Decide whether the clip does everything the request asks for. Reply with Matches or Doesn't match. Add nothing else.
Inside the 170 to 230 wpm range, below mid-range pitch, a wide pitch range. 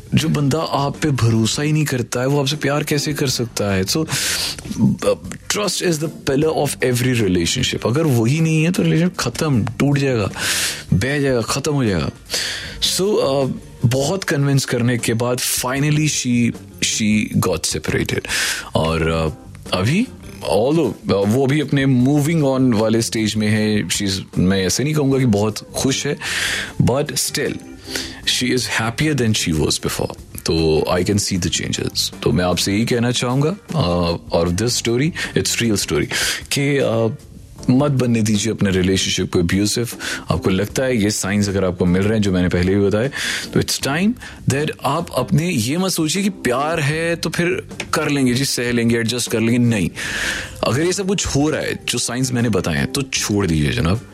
Matches